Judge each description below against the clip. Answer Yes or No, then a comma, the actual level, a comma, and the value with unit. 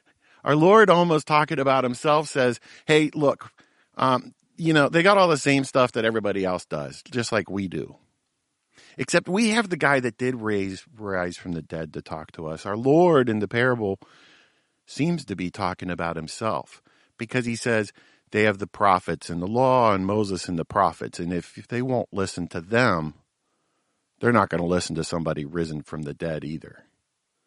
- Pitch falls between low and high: No, low, 110 Hz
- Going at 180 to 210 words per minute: Yes, average, 190 wpm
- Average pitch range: No, wide, 7.8 semitones